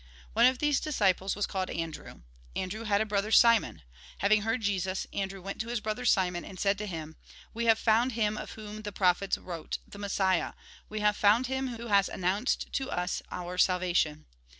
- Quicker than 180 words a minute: Yes, average, 195 wpm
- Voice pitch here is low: No, high, 205 Hz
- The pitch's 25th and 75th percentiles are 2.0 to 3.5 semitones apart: Yes, average, 3.2 semitones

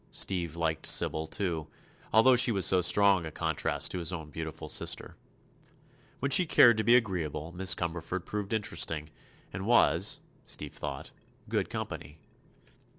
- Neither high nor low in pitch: No, very low, 90 Hz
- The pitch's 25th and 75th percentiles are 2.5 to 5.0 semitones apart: Yes, average, 4.3 semitones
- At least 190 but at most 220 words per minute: No, average, 150 wpm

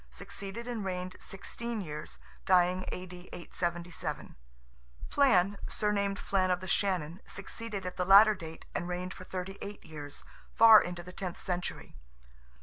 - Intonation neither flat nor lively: No, narrow, 2.1 semitones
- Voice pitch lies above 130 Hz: Yes, medium, 185 Hz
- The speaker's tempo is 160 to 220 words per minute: No, average, 145 wpm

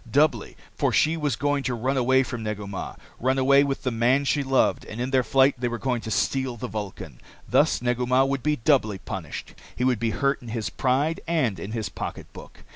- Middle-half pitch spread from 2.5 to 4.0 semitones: Yes, average, 3.4 semitones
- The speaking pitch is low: Yes, low, 125 Hz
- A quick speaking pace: Yes, fast, 220 wpm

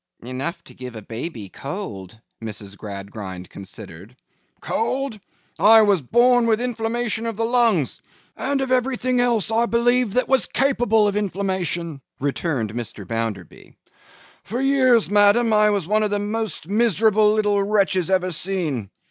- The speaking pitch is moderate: No, high, 205 Hz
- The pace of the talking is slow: No, average, 145 wpm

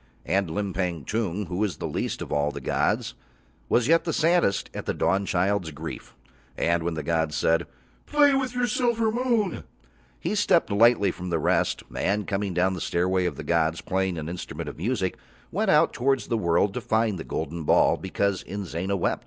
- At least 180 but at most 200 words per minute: Yes, average, 185 wpm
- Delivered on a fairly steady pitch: No, wide, 5.6 semitones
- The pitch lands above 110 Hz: No, very low, 95 Hz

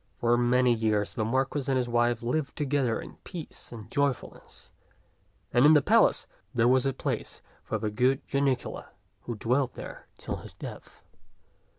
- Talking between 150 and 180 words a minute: Yes, average, 165 wpm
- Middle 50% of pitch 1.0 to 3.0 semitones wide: Yes, narrow, 2.5 semitones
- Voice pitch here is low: Yes, low, 125 Hz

